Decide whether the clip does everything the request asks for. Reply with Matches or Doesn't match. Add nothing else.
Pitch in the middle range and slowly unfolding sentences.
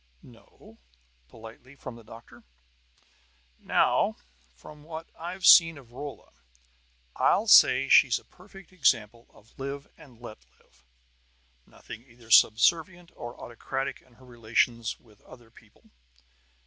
Doesn't match